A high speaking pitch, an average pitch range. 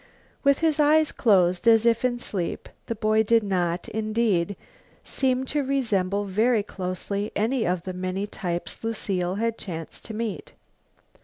Yes: high, 215 Hz; average, 4.1 semitones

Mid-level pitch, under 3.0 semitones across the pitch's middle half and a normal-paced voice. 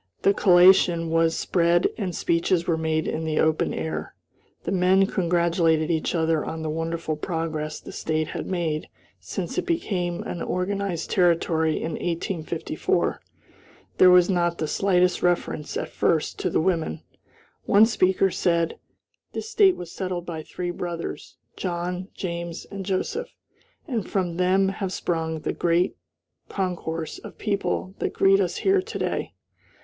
Yes: medium, 175 Hz; narrow, 2.4 semitones; average, 150 wpm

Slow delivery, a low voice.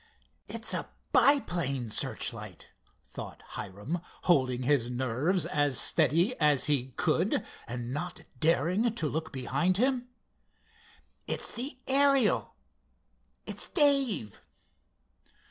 No: slow, 95 wpm; medium, 160 Hz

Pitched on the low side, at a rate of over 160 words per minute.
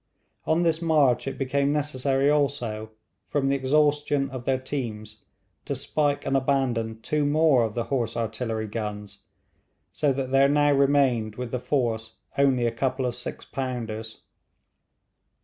No: low, 130 Hz; average, 150 wpm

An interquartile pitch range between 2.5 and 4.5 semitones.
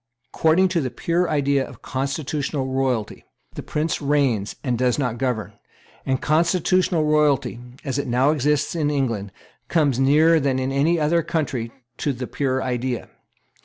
Yes: average, 3.1 semitones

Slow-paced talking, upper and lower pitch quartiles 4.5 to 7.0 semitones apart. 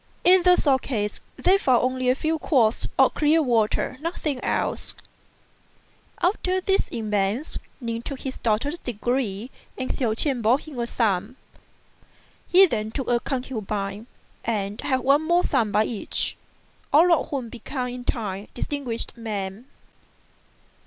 No: average, 145 wpm; average, 4.8 semitones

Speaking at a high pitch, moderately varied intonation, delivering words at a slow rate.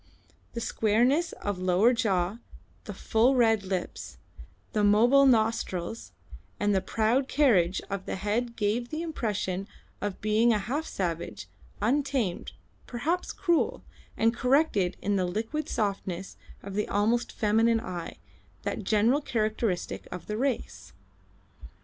Yes: high, 220 Hz; average, 3.7 semitones; slow, 125 wpm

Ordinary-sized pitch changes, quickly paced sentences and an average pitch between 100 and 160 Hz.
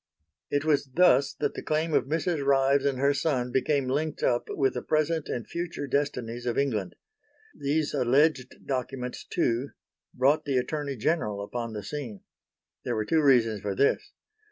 No: average, 3.3 semitones; average, 165 wpm; medium, 140 Hz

